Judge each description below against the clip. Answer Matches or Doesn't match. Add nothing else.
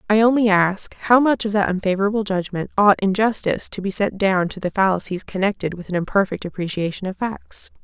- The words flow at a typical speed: Matches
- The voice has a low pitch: Doesn't match